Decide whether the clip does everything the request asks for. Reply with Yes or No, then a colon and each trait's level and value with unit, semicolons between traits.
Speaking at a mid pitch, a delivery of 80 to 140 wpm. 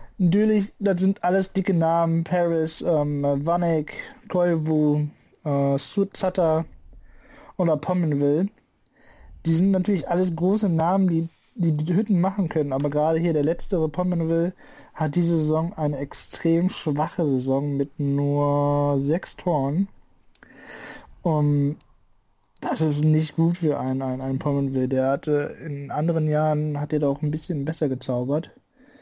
Yes: medium, 160 Hz; average, 135 wpm